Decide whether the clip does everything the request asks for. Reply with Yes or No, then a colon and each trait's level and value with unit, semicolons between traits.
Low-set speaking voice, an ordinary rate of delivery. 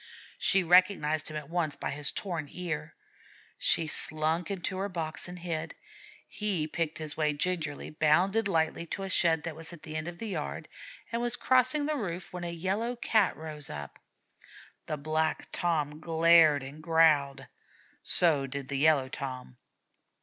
No: medium, 160 Hz; average, 165 wpm